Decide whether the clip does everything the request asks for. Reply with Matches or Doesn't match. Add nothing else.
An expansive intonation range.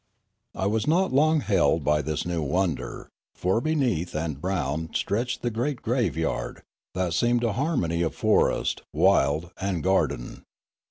Matches